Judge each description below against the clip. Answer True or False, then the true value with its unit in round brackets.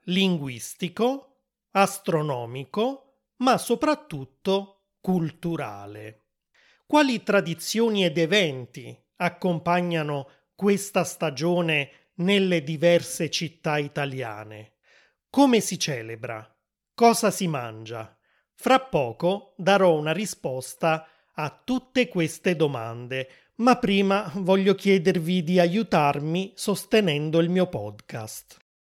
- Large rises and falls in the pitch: True (5.7 semitones)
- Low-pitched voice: False (175 Hz)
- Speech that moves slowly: True (85 wpm)